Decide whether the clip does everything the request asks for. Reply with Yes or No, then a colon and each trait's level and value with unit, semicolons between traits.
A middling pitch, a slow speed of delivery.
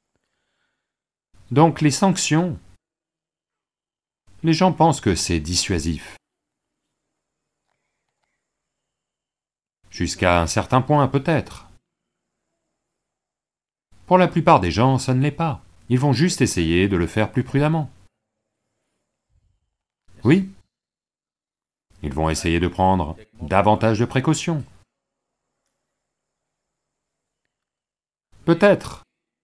No: low, 115 Hz; slow, 85 wpm